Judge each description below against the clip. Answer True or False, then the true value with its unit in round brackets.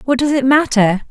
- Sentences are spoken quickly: True (215 wpm)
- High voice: True (255 Hz)